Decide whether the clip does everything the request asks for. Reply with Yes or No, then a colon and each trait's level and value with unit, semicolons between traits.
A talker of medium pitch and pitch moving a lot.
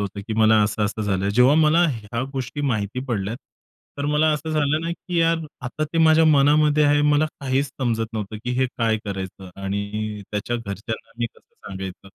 No: low, 120 Hz; wide, 6.1 semitones